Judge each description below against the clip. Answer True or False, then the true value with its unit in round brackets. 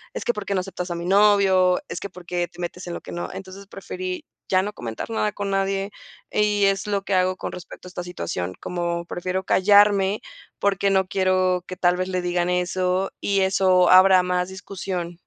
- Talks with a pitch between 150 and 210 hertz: True (185 Hz)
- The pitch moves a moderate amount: False (1.6 semitones)